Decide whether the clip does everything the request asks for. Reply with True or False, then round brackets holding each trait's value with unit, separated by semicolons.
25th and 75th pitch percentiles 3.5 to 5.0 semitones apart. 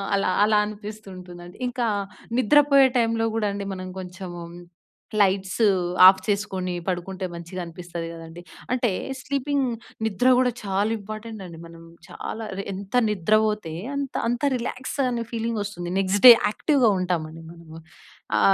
True (4.3 semitones)